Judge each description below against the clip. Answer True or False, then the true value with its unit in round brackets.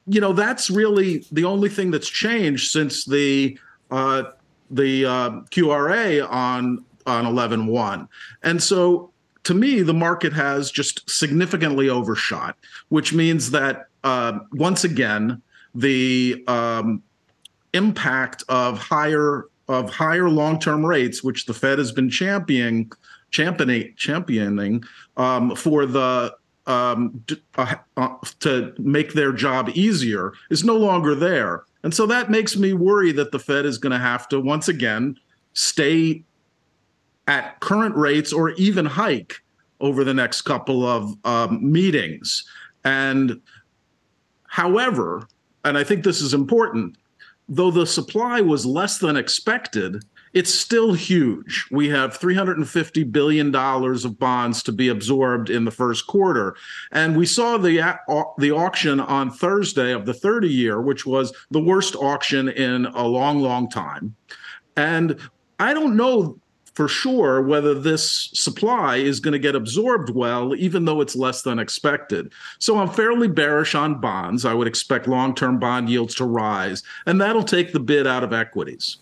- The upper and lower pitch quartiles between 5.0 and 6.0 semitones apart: True (5.4 semitones)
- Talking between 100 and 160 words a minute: True (150 wpm)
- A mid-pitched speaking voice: True (145 Hz)